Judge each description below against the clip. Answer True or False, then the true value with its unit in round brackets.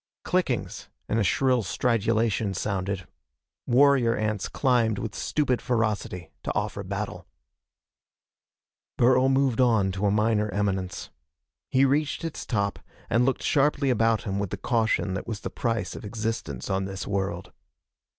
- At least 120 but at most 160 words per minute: True (140 wpm)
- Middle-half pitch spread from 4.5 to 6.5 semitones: False (3.9 semitones)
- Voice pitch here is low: True (110 Hz)